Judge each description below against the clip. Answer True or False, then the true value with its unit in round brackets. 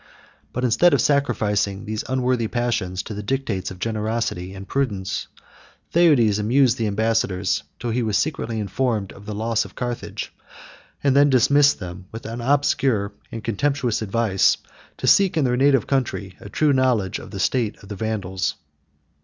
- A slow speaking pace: False (160 wpm)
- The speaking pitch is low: True (115 Hz)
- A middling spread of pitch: True (4.3 semitones)